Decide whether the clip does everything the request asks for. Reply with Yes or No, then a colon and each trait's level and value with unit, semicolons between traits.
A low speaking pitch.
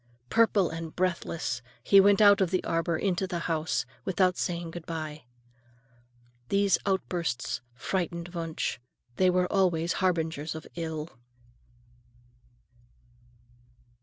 No: medium, 170 Hz